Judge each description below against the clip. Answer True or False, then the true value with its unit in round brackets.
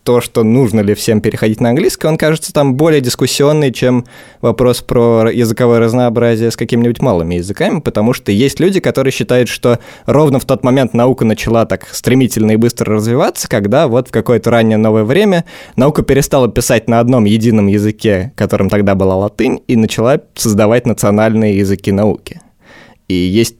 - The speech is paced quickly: True (170 wpm)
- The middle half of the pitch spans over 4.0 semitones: False (2.8 semitones)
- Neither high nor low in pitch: False (115 Hz)